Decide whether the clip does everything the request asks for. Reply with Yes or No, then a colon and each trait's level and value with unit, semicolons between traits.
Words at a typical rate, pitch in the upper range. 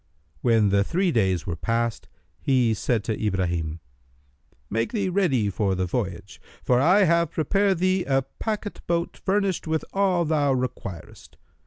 No: average, 150 wpm; low, 130 Hz